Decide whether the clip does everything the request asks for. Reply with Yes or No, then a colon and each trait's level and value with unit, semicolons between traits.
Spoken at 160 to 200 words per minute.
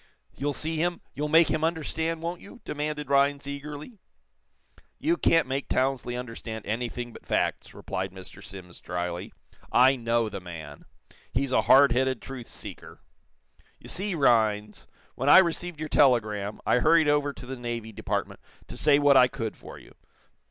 Yes: average, 165 wpm